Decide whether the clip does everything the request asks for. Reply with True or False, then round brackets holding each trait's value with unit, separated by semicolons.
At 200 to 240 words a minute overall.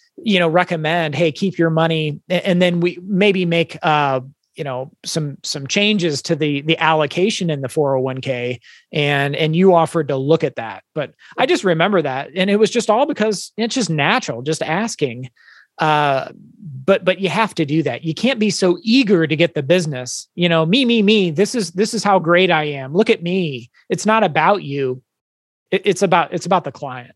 True (205 wpm)